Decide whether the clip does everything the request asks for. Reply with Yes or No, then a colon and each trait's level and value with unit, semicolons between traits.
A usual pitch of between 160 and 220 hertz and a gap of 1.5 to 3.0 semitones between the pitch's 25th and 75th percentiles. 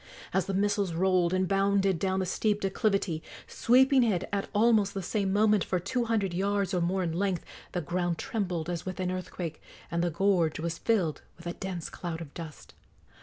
Yes: high, 190 Hz; narrow, 2.6 semitones